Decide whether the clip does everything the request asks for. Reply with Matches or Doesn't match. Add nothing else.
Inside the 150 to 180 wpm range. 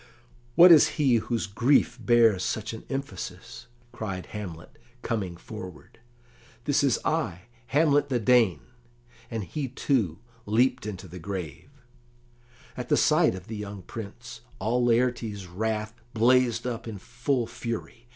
Doesn't match